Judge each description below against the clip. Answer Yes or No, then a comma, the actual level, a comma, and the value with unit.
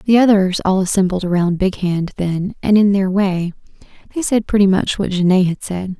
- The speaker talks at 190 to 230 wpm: Yes, average, 200 wpm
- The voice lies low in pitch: No, high, 190 Hz